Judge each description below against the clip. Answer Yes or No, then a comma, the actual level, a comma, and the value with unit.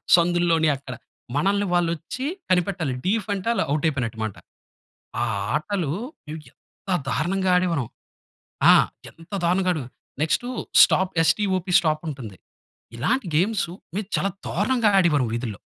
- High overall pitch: No, medium, 175 Hz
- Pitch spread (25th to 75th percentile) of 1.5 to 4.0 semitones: No, average, 4.5 semitones